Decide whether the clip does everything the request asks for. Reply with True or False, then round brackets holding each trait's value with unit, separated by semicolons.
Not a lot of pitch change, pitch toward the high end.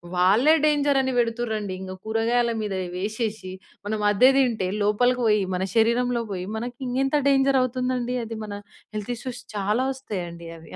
False (3.3 semitones; 230 Hz)